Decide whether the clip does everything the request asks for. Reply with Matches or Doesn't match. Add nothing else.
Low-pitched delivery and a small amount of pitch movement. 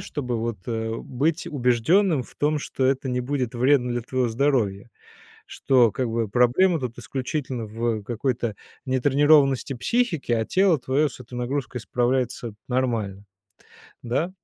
Doesn't match